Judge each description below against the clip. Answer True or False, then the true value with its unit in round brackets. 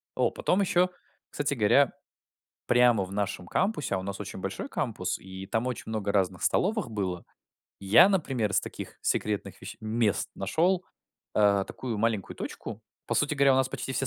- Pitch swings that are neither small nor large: False (5.9 semitones)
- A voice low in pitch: True (115 Hz)